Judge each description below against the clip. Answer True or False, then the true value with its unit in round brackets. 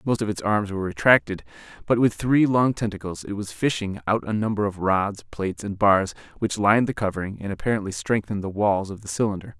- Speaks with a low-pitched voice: True (100 Hz)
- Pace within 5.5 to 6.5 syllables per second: True (6.0 syllables/s)